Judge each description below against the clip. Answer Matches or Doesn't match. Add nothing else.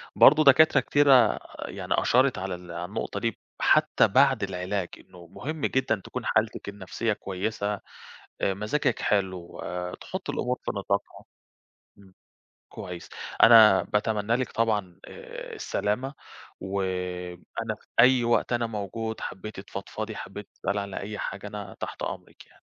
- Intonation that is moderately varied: Matches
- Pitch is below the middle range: Matches